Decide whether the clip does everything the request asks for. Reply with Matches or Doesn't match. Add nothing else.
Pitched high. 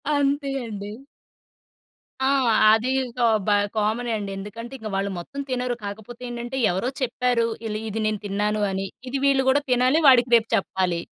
Matches